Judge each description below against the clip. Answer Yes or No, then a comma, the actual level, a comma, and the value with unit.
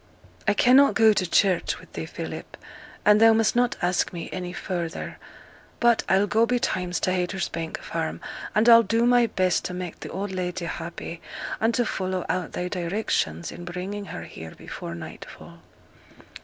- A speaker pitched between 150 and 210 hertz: Yes, medium, 185 Hz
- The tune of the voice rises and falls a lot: No, average, 4.0 semitones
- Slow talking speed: No, average, 170 wpm